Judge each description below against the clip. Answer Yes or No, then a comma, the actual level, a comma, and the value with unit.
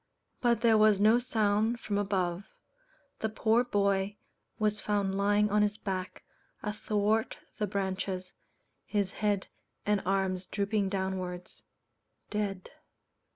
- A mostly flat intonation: Yes, narrow, 1.8 semitones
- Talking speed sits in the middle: No, slow, 115 wpm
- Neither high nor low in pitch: No, high, 205 Hz